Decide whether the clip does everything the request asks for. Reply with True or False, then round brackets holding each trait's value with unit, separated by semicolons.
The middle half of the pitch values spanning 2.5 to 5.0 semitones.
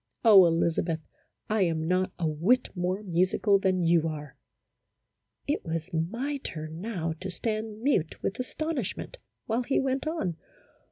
False (5.5 semitones)